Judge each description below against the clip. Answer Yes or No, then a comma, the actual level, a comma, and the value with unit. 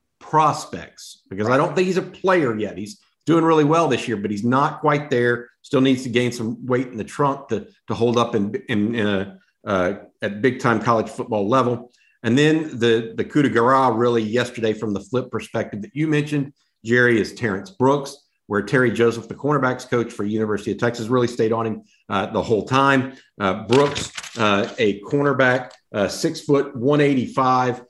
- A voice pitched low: Yes, low, 125 Hz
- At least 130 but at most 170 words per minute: No, average, 200 wpm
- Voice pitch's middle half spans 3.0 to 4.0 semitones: Yes, average, 3.6 semitones